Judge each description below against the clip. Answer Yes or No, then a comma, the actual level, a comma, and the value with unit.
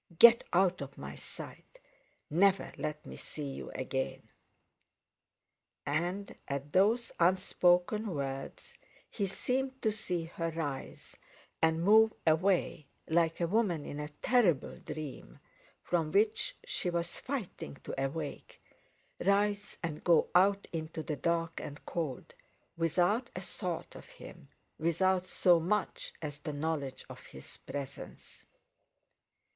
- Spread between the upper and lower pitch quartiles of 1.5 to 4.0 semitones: No, average, 4.5 semitones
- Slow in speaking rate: Yes, slow, 125 wpm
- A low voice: No, medium, 170 Hz